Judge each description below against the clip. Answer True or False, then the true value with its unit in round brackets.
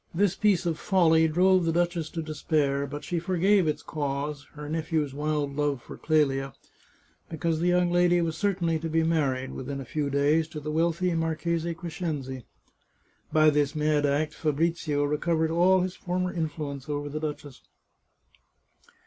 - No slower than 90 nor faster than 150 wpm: False (165 wpm)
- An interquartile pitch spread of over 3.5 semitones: False (2.7 semitones)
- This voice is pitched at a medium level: True (155 Hz)